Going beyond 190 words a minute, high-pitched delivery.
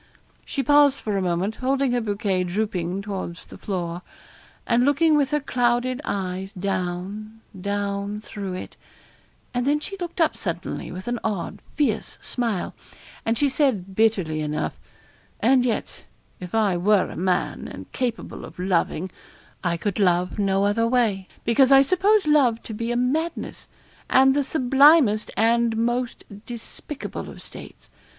No: average, 155 wpm; high, 220 Hz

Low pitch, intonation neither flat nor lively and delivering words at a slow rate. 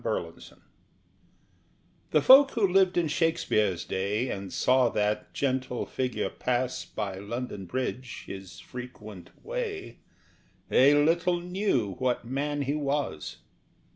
No: low, 130 Hz; wide, 7.6 semitones; slow, 120 wpm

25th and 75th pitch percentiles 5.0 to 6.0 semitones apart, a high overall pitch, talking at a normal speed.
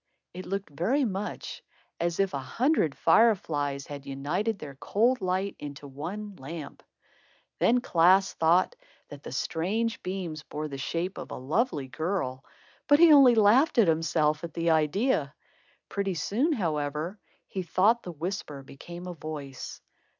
No: wide, 5.5 semitones; medium, 175 Hz; average, 150 wpm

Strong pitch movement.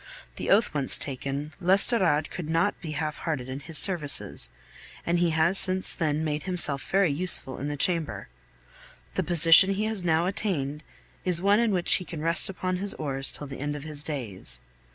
No: average, 4.0 semitones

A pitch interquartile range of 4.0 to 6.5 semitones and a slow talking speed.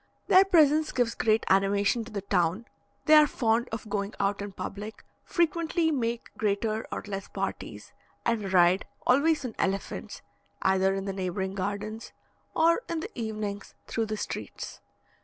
No: average, 4.4 semitones; average, 155 wpm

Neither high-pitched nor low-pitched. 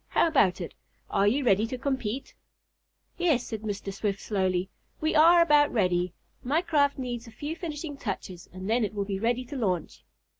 No: high, 235 Hz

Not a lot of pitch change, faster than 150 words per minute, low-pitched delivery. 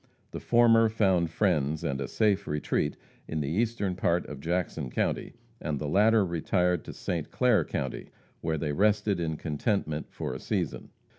No: wide, 5.4 semitones; average, 165 wpm; very low, 85 Hz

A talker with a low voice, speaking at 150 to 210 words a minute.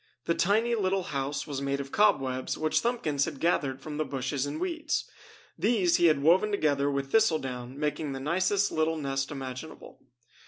No: medium, 150 Hz; average, 175 wpm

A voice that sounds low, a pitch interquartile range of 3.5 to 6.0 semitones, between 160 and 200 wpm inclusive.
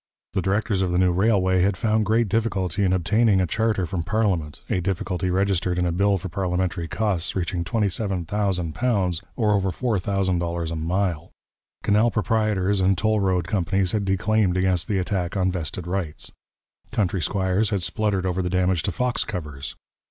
No: very low, 95 Hz; narrow, 2.6 semitones; average, 165 wpm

